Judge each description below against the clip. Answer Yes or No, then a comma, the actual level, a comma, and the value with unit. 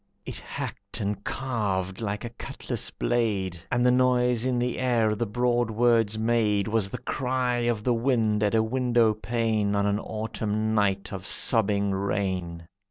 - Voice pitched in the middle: No, low, 110 Hz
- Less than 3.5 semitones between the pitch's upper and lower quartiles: Yes, average, 3.0 semitones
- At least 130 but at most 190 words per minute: Yes, average, 165 wpm